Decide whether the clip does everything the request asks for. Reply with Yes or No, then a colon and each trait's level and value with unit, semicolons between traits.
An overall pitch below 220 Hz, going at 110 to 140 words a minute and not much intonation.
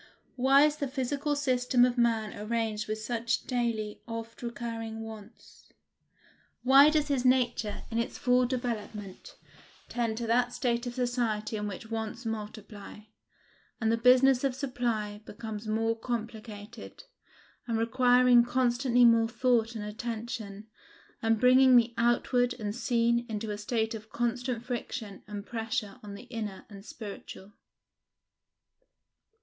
No: high, 230 Hz; slow, 135 wpm; narrow, 2.2 semitones